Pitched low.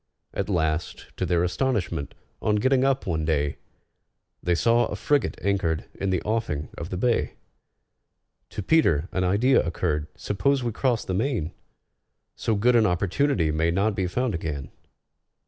Yes: very low, 95 Hz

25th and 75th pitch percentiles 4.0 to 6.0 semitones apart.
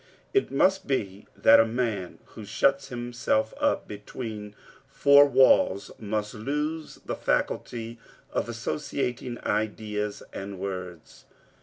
Yes: average, 4.3 semitones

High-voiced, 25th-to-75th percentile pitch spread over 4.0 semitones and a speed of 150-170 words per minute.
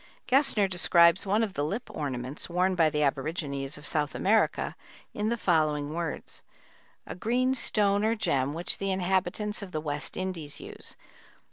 No: medium, 175 Hz; wide, 5.4 semitones; average, 160 wpm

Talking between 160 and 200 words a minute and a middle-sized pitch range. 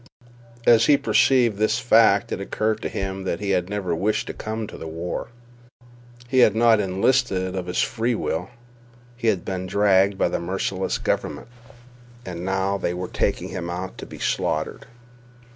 Yes: average, 175 wpm; average, 3.2 semitones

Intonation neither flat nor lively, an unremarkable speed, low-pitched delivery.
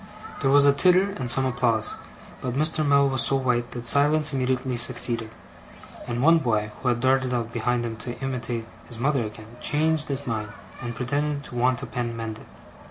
Yes: average, 3.0 semitones; average, 190 wpm; low, 125 Hz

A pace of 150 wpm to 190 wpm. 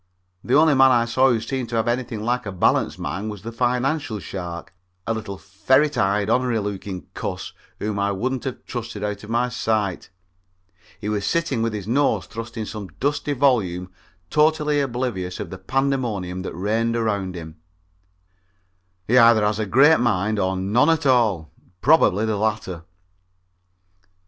Yes: average, 165 wpm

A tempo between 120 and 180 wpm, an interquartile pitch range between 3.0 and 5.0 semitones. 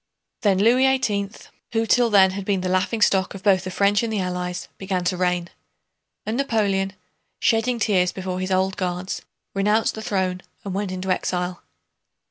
No: average, 170 wpm; narrow, 2.5 semitones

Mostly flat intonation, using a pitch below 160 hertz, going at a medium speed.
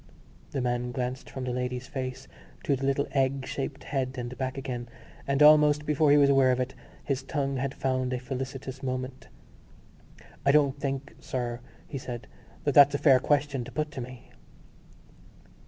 Yes: narrow, 1.6 semitones; low, 135 Hz; average, 175 wpm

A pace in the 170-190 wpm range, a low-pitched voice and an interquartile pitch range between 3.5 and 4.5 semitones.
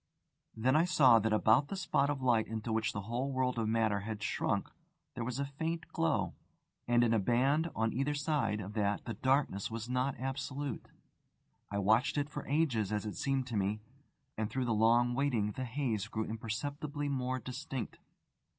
Yes: average, 185 wpm; low, 120 Hz; average, 4.1 semitones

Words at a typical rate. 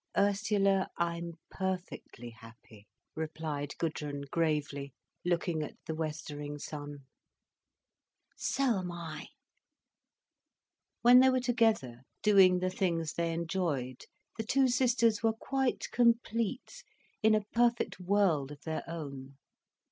No: slow, 110 wpm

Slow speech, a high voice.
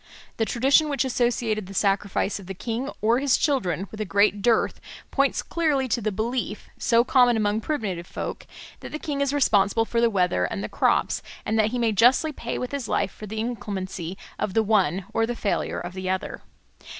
No: fast, 205 wpm; high, 220 Hz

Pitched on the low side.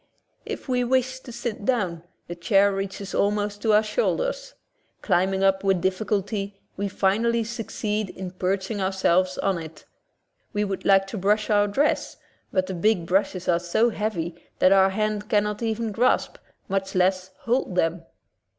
No: high, 200 Hz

